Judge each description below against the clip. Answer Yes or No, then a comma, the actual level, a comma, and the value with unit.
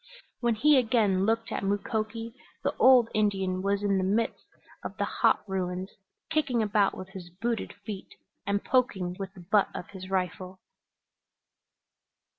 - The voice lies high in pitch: Yes, high, 200 Hz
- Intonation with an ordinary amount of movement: Yes, average, 3.2 semitones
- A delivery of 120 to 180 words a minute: Yes, average, 150 wpm